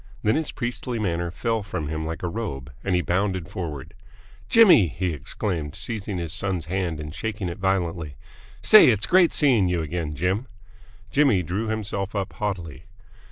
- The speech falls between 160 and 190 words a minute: Yes, average, 165 wpm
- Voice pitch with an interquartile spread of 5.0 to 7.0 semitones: No, average, 4.5 semitones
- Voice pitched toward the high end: No, very low, 95 Hz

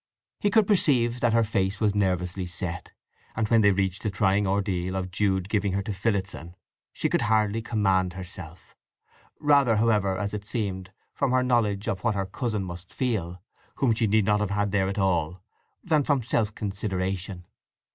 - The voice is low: Yes, low, 100 Hz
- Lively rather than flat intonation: No, average, 2.9 semitones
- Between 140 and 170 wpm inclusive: No, average, 180 wpm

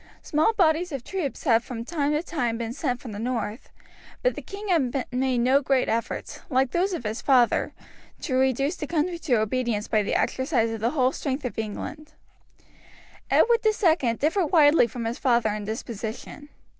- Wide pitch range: No, average, 5.0 semitones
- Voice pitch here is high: Yes, very high, 260 Hz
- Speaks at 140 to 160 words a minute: No, average, 180 wpm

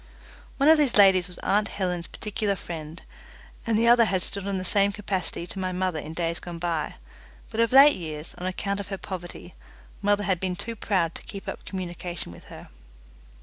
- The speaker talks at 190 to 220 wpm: Yes, average, 200 wpm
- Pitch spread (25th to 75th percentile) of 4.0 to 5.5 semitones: No, average, 2.8 semitones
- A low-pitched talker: No, high, 190 Hz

